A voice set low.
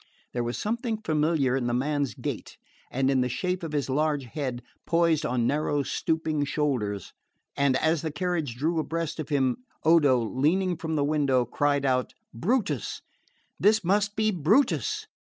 No: medium, 150 Hz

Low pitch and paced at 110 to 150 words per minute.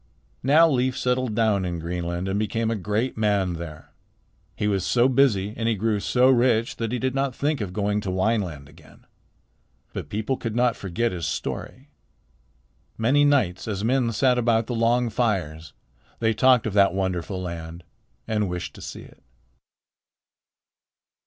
No: low, 110 Hz; average, 165 wpm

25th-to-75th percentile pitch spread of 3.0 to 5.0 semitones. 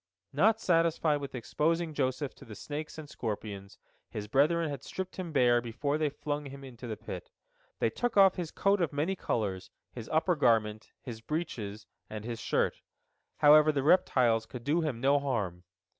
No: wide, 5.5 semitones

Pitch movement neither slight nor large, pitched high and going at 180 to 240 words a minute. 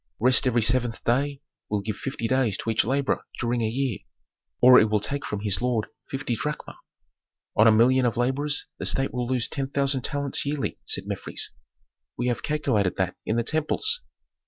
No: average, 3.4 semitones; low, 125 Hz; average, 185 wpm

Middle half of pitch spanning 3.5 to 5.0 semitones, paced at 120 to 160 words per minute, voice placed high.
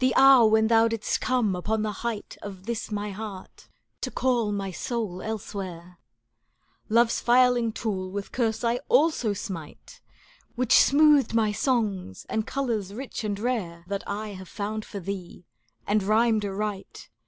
No: average, 3.0 semitones; average, 155 wpm; high, 215 Hz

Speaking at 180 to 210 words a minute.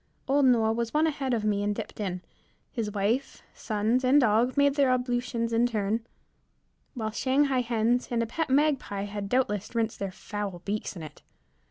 Yes: average, 185 wpm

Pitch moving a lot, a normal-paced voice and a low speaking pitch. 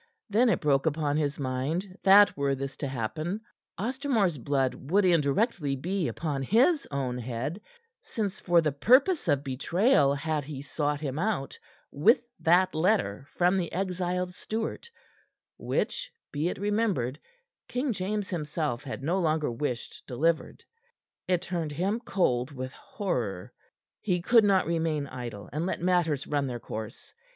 No: wide, 5.7 semitones; average, 145 wpm; medium, 160 Hz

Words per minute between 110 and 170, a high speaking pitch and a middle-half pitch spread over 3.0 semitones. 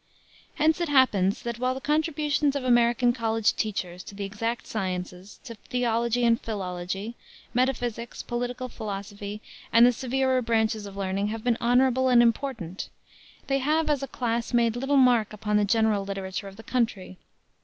Yes: average, 165 wpm; high, 230 Hz; average, 3.8 semitones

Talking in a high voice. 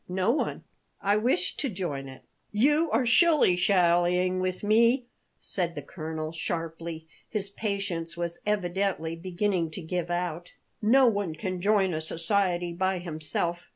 No: medium, 180 Hz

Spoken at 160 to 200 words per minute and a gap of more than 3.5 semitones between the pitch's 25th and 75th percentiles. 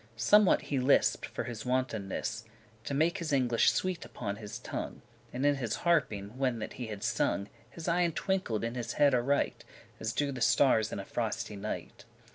Yes: average, 190 wpm; average, 4.6 semitones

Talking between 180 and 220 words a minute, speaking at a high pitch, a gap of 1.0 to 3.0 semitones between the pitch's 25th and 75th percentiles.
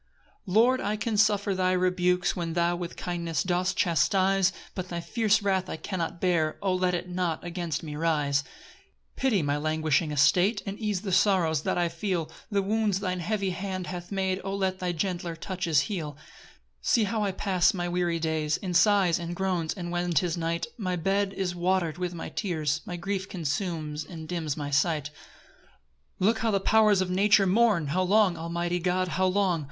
No: average, 195 wpm; medium, 180 Hz; average, 2.7 semitones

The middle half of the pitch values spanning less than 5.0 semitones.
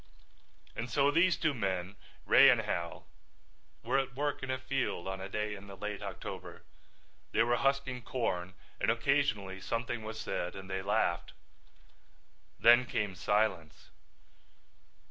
No: average, 5.3 semitones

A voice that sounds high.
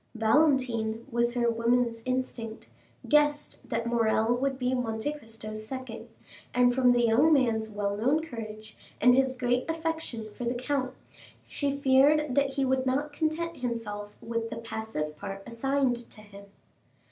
Yes: high, 245 Hz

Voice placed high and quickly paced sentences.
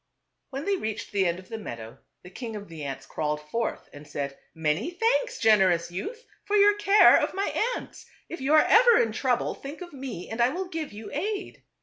Yes: high, 235 Hz; fast, 220 wpm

